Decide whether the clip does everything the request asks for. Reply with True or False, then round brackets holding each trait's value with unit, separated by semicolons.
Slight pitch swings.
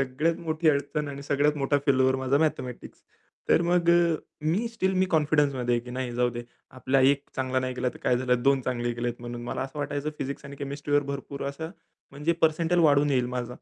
False (3.0 semitones)